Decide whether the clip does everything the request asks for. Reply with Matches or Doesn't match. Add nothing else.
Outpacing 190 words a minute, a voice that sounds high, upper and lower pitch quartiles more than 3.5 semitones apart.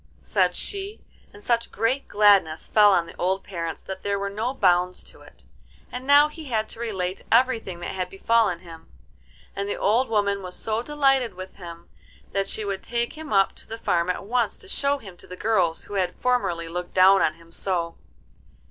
Matches